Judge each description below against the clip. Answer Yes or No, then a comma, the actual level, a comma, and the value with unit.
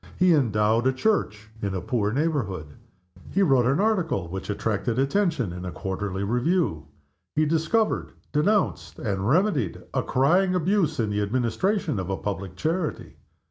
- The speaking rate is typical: Yes, average, 150 wpm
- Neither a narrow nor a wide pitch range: No, wide, 8.9 semitones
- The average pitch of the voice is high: No, low, 125 Hz